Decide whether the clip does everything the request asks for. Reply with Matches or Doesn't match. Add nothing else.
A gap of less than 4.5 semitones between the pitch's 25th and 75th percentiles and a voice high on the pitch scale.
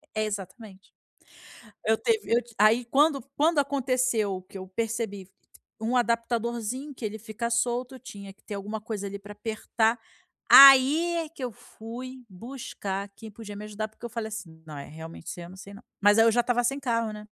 Matches